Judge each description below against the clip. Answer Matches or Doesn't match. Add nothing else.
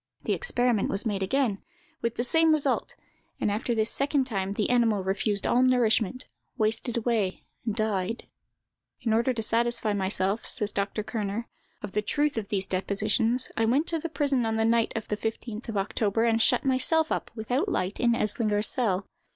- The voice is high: Matches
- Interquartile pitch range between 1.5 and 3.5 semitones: Matches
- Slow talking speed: Doesn't match